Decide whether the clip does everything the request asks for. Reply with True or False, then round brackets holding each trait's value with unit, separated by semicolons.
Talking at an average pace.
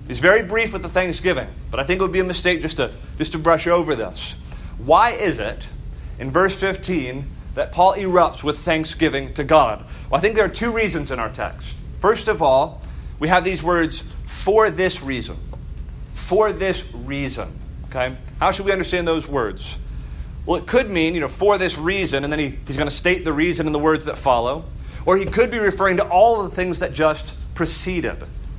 False (210 wpm)